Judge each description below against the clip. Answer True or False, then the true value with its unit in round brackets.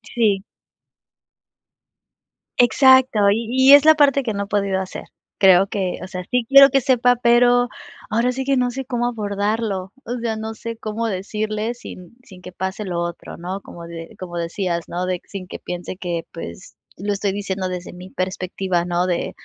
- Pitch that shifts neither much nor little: True (4.7 semitones)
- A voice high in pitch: True (205 Hz)